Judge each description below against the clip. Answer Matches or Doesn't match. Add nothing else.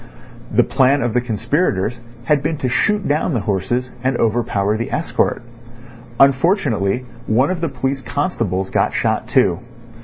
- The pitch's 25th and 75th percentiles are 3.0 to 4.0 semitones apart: Doesn't match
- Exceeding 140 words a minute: Matches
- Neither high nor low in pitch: Doesn't match